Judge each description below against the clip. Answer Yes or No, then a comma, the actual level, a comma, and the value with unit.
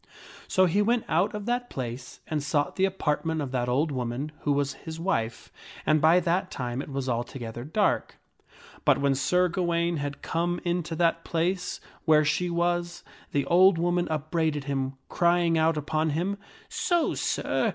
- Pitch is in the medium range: Yes, medium, 160 Hz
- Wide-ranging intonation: No, average, 3.8 semitones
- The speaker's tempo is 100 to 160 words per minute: No, average, 180 wpm